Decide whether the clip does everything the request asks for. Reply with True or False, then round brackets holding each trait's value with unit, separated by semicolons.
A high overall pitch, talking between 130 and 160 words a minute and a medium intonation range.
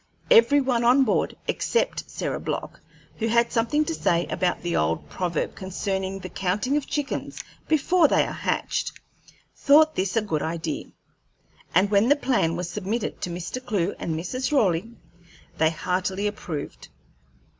False (200 Hz; 155 wpm; 6.6 semitones)